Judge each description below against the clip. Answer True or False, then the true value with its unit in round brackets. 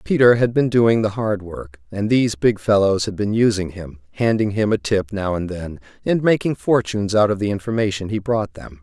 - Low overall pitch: True (105 Hz)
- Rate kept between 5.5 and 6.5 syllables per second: False (5.3 syllables/s)